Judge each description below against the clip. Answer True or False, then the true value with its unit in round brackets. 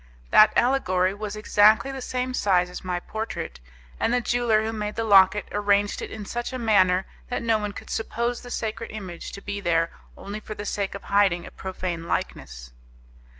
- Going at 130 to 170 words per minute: False (195 wpm)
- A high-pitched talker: True (210 Hz)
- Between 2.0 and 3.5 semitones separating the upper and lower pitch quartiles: True (3.1 semitones)